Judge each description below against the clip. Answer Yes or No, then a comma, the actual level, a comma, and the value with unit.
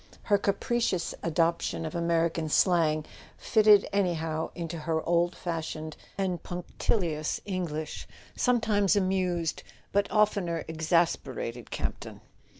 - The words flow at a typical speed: No, slow, 110 wpm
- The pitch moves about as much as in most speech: Yes, average, 3.2 semitones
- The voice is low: No, medium, 170 Hz